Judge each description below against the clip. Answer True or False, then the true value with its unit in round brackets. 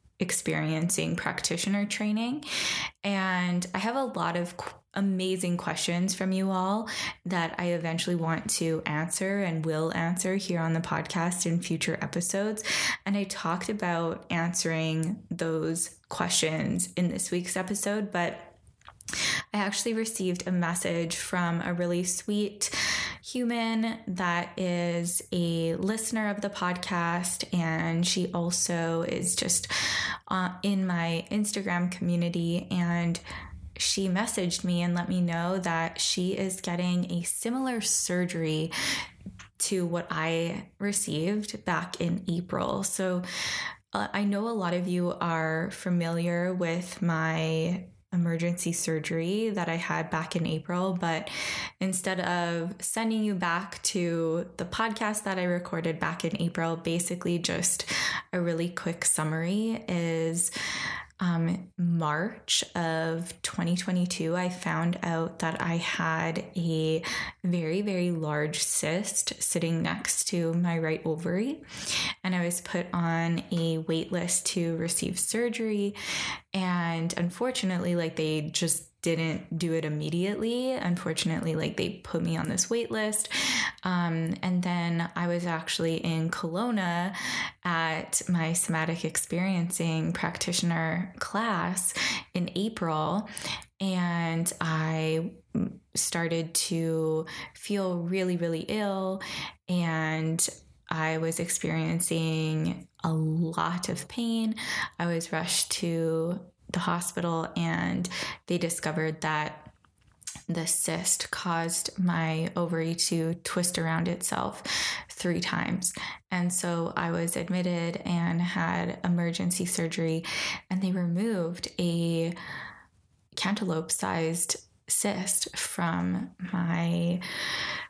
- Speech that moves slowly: True (120 wpm)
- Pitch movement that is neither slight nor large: False (2.2 semitones)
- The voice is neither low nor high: True (175 Hz)